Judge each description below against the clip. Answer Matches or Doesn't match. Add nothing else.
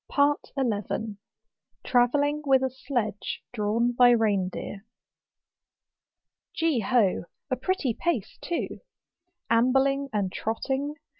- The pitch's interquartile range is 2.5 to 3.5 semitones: Doesn't match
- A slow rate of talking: Matches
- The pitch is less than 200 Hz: Doesn't match